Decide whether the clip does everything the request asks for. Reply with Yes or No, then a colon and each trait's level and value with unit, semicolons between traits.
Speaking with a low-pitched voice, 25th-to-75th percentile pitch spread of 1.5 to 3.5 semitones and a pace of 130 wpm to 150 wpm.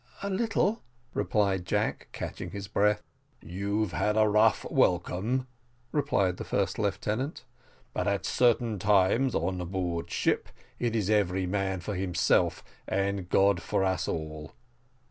Yes: low, 100 Hz; average, 2.8 semitones; average, 140 wpm